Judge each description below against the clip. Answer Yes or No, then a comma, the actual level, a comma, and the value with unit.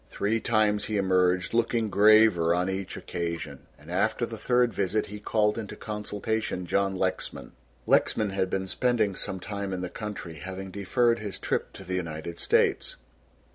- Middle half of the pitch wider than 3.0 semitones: No, average, 2.7 semitones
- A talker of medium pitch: No, low, 100 Hz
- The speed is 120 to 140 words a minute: No, average, 165 wpm